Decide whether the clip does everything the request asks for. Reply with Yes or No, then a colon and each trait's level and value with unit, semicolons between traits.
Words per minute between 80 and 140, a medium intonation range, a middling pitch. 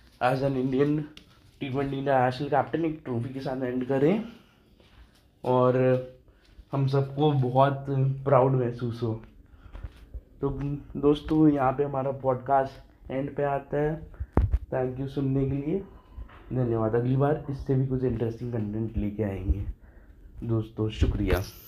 No: average, 135 wpm; average, 4.0 semitones; low, 130 Hz